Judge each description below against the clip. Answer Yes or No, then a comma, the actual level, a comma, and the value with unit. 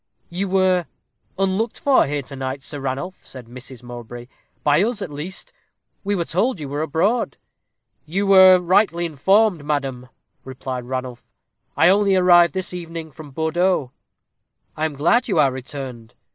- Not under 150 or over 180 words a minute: Yes, average, 155 wpm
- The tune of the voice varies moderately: No, wide, 5.8 semitones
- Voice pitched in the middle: Yes, medium, 160 Hz